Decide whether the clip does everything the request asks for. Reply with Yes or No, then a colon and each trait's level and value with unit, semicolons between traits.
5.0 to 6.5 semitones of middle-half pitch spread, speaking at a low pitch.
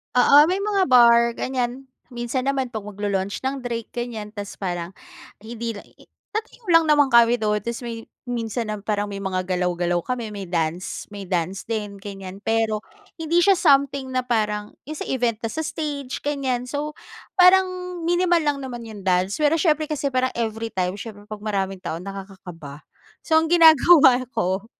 No: wide, 5.5 semitones; high, 235 Hz